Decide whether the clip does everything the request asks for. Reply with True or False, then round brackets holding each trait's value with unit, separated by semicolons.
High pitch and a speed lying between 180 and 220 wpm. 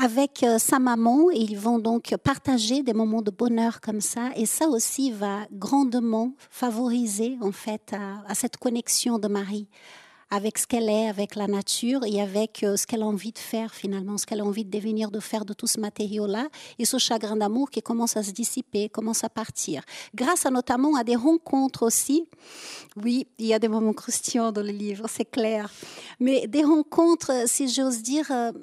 True (230 Hz; 195 wpm)